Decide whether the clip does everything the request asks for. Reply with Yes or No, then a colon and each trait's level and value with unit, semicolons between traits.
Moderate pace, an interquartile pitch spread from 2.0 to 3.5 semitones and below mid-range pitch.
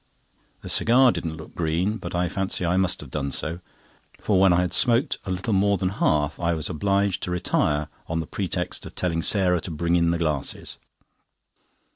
Yes: average, 195 wpm; average, 3.0 semitones; very low, 90 Hz